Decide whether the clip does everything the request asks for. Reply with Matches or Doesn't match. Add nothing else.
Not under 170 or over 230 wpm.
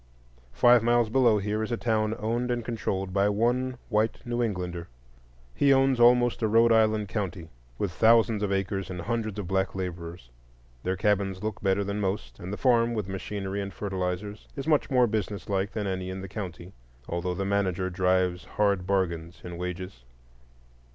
Matches